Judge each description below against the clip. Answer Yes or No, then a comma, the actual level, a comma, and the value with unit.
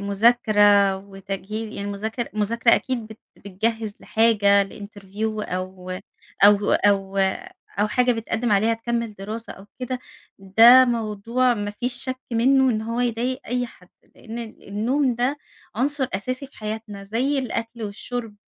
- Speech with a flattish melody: No, average, 3.1 semitones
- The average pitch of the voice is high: Yes, high, 220 Hz